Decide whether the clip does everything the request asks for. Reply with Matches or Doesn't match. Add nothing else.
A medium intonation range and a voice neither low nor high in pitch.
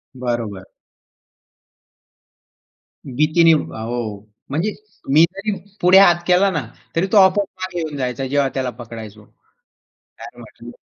Doesn't match